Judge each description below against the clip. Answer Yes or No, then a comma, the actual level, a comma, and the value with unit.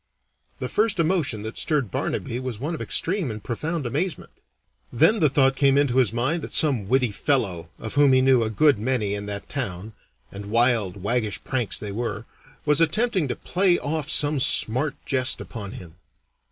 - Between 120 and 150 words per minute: No, average, 180 wpm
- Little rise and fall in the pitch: No, wide, 5.4 semitones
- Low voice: Yes, low, 130 Hz